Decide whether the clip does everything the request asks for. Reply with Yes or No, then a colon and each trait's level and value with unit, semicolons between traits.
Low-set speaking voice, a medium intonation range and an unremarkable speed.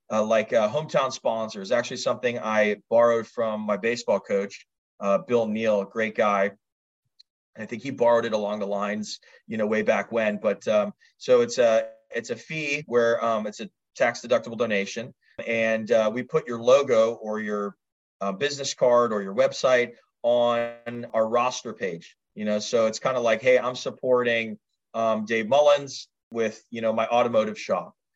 No: low, 115 Hz; narrow, 2.2 semitones; average, 180 wpm